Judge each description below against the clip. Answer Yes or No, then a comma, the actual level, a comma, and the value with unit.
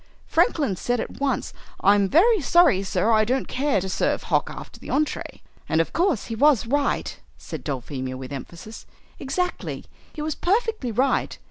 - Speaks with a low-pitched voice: No, very high, 250 Hz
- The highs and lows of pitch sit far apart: Yes, wide, 7.8 semitones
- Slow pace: No, average, 165 wpm